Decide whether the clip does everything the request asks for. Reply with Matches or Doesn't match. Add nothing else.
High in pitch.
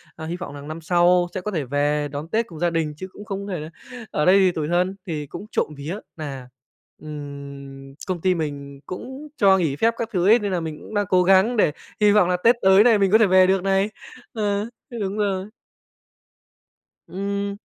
Doesn't match